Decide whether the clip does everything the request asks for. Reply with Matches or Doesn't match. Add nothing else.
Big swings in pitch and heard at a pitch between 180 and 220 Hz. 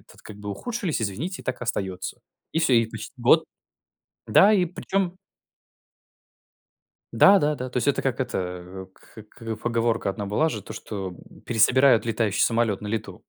Doesn't match